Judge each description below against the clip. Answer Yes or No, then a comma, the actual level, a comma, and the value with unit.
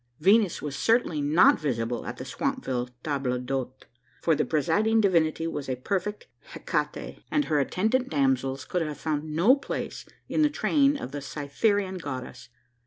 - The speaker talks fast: No, average, 160 wpm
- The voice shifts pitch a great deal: Yes, wide, 7.3 semitones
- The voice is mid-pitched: Yes, medium, 155 Hz